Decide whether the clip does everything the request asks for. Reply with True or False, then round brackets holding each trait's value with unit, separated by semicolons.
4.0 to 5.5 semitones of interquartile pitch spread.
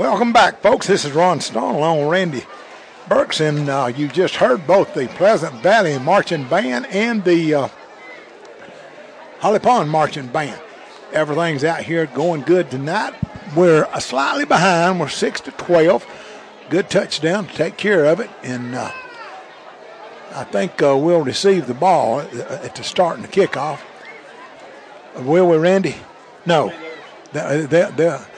False (3.5 semitones)